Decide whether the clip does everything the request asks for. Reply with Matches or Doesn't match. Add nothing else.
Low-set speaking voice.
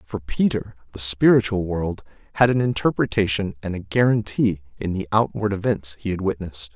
Matches